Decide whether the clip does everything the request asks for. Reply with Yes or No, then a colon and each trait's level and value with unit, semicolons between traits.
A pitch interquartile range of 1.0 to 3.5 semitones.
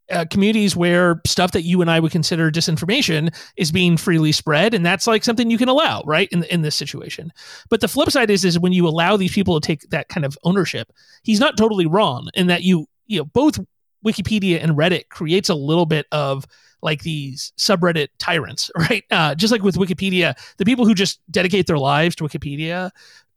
No: average, 3.9 semitones